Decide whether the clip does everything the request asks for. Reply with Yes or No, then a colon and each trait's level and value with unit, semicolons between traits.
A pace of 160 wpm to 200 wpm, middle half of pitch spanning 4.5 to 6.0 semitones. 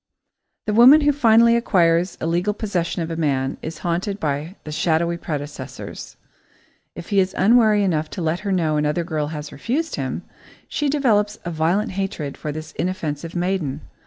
Yes: average, 165 wpm; average, 4.8 semitones